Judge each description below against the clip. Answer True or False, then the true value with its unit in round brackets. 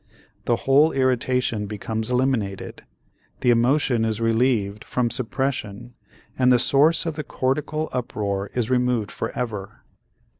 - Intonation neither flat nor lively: True (3.1 semitones)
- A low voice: True (125 Hz)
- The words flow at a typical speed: False (120 wpm)